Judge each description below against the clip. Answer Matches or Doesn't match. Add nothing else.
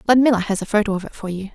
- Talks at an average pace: Doesn't match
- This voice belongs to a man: Doesn't match